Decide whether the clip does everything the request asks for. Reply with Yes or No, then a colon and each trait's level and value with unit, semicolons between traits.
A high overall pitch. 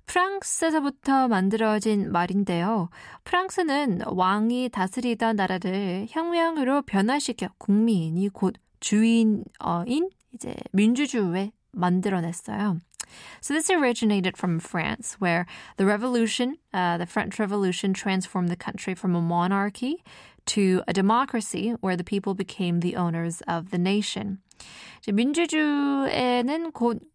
Yes: high, 205 Hz